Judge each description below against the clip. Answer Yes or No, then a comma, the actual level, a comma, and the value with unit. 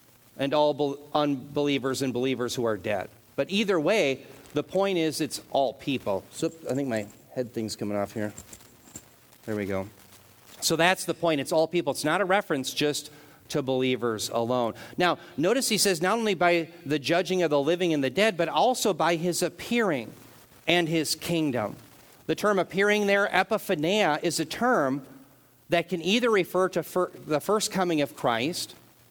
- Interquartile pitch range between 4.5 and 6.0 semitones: Yes, wide, 5.6 semitones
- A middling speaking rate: Yes, average, 175 wpm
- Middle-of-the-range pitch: Yes, medium, 150 Hz